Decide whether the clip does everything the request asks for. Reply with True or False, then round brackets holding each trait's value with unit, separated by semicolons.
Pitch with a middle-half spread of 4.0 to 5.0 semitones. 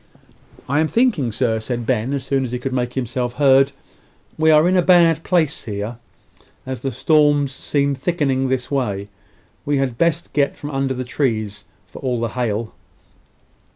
False (3.2 semitones)